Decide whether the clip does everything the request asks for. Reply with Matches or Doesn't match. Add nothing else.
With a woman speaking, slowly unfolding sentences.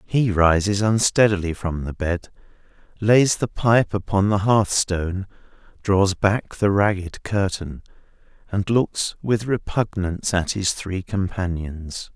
Doesn't match